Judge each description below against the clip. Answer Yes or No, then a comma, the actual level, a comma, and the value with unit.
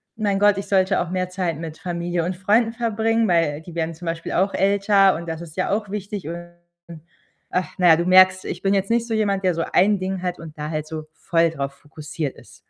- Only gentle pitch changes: No, average, 3.1 semitones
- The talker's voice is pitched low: No, medium, 185 Hz